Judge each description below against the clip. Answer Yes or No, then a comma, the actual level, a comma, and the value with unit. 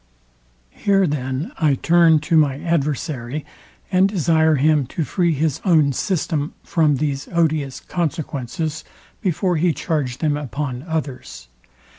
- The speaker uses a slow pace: Yes, slow, 125 wpm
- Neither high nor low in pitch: Yes, medium, 155 Hz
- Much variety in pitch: No, average, 3.1 semitones